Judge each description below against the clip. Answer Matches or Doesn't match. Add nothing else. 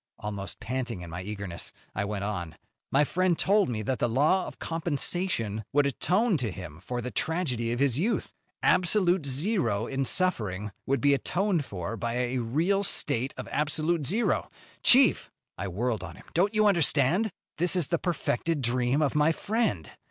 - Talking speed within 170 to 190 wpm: Matches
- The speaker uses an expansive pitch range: Matches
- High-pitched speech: Doesn't match